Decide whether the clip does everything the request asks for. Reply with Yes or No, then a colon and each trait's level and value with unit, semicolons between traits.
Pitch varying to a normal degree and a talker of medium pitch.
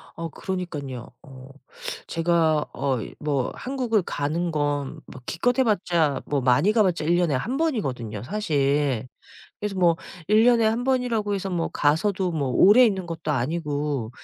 No: wide, 6.5 semitones; medium, 165 Hz